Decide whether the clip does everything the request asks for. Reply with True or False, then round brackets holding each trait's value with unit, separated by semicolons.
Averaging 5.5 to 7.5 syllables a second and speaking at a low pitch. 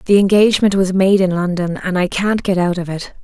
False (5.7 syllables/s; 185 Hz)